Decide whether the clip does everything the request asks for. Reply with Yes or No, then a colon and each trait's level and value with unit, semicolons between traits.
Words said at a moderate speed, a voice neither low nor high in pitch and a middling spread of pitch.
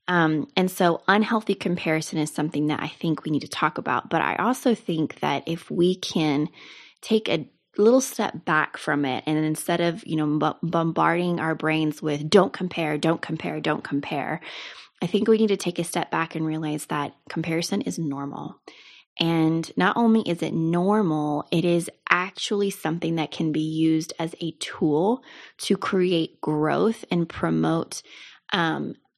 Yes: average, 175 wpm; medium, 165 Hz; average, 3.0 semitones